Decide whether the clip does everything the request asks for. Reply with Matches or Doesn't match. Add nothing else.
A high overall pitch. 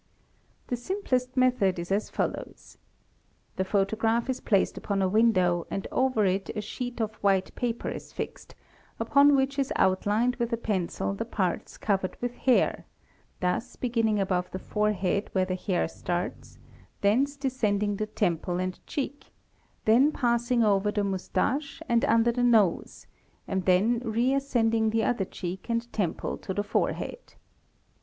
Matches